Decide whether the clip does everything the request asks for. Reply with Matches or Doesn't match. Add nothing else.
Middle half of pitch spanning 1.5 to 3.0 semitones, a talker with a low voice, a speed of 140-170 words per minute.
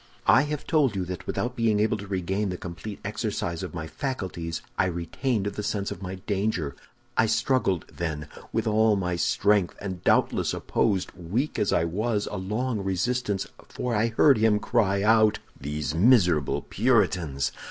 Doesn't match